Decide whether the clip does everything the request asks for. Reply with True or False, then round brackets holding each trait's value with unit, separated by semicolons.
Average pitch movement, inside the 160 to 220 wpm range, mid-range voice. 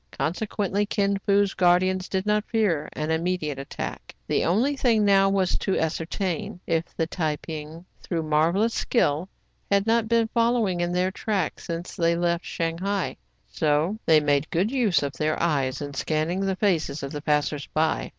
True (4.3 semitones; 170 wpm; 175 Hz)